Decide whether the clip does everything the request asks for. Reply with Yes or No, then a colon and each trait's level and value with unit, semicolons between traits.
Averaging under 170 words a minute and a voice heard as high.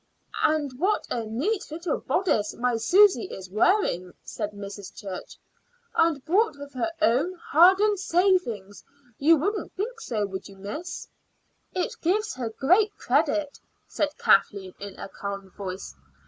Yes: average, 145 wpm; very high, 285 Hz